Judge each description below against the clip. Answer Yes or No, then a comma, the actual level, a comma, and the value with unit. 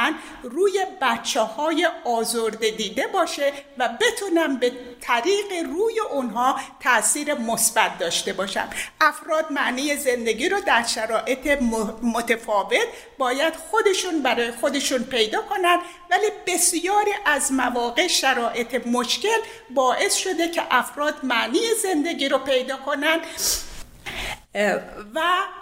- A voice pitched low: No, very high, 290 Hz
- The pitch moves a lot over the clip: Yes, wide, 6.4 semitones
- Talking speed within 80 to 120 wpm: Yes, slow, 105 wpm